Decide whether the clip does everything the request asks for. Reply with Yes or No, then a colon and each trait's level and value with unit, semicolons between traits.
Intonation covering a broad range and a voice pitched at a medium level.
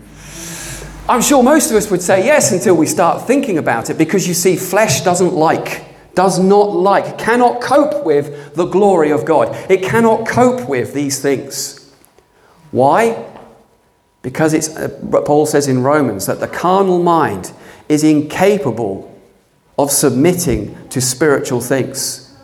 Yes: wide, 6.1 semitones; medium, 165 Hz